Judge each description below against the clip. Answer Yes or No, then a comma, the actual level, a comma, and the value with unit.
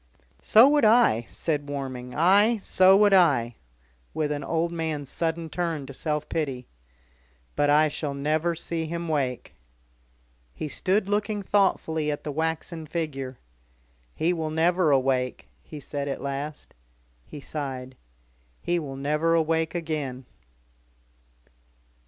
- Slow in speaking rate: Yes, slow, 130 wpm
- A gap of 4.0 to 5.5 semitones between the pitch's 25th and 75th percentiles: No, average, 3.3 semitones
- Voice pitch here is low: No, medium, 155 Hz